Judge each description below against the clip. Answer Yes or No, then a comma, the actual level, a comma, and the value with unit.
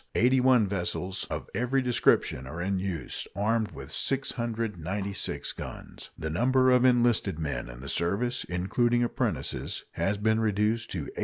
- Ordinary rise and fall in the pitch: Yes, average, 4.8 semitones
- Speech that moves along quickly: No, average, 150 wpm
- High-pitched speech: No, low, 105 Hz